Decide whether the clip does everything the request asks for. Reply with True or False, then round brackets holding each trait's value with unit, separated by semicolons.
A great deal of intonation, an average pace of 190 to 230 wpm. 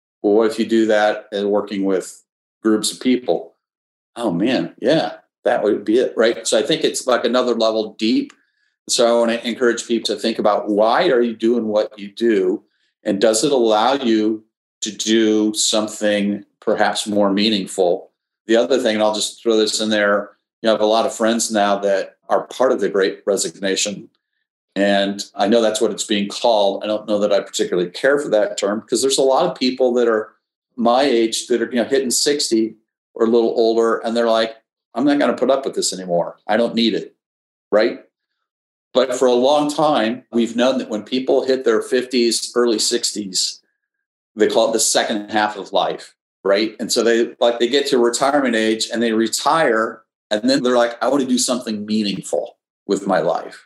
False (2.8 semitones; 205 wpm)